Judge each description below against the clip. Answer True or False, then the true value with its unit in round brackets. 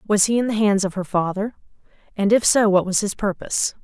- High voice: True (205 Hz)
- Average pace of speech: False (235 wpm)